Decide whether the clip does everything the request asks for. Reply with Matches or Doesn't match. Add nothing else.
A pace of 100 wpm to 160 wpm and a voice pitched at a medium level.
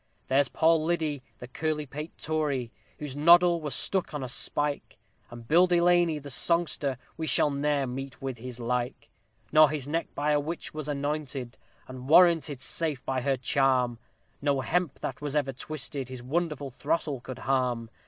Doesn't match